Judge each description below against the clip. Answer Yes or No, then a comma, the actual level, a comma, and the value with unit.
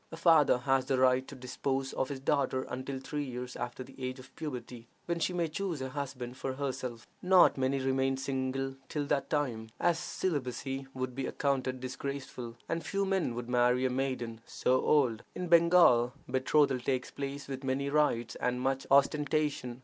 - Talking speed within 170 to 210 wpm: Yes, average, 180 wpm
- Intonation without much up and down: Yes, narrow, 2.1 semitones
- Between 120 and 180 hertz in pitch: Yes, low, 135 Hz